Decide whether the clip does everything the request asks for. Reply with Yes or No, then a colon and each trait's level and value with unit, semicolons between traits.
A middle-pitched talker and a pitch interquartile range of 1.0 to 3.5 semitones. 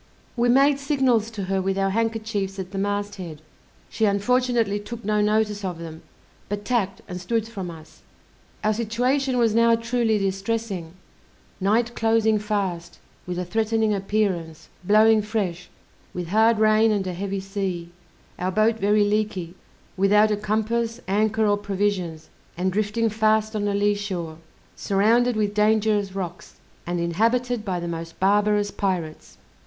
No: high, 205 Hz; average, 2.7 semitones